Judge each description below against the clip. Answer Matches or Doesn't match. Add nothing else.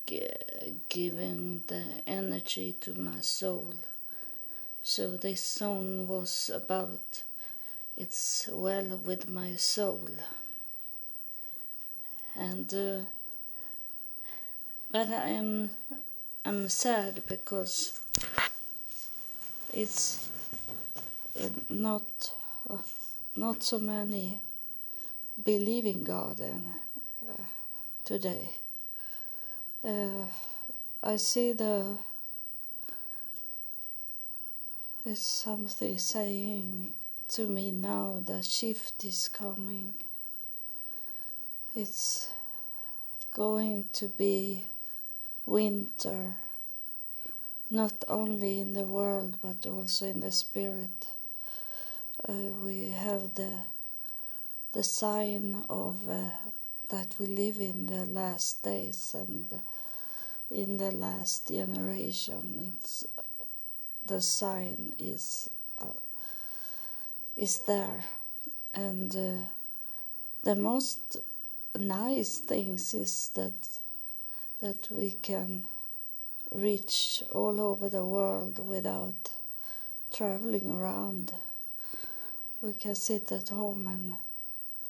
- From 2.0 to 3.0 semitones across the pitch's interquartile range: Matches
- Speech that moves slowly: Matches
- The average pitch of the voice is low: Doesn't match